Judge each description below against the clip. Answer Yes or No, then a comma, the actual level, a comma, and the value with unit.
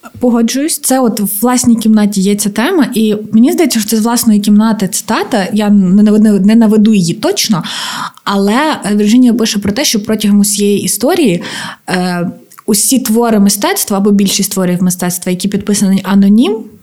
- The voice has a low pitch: No, high, 210 Hz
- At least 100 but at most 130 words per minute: No, average, 145 wpm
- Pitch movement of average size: No, narrow, 2.3 semitones